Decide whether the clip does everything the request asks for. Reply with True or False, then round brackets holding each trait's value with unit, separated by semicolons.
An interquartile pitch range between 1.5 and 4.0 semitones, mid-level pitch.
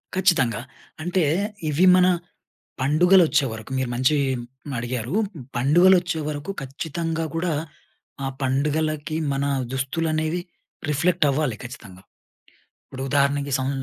True (3.7 semitones; 150 Hz)